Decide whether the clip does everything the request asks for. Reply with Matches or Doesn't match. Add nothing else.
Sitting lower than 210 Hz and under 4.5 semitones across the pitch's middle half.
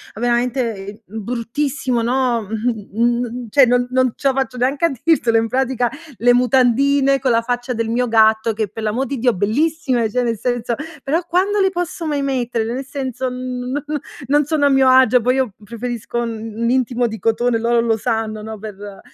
Doesn't match